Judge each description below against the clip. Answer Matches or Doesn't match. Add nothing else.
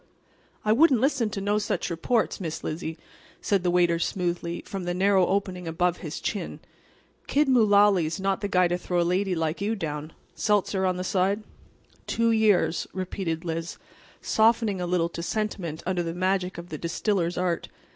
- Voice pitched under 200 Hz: Matches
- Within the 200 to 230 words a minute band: Doesn't match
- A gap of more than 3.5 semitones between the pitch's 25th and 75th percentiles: Doesn't match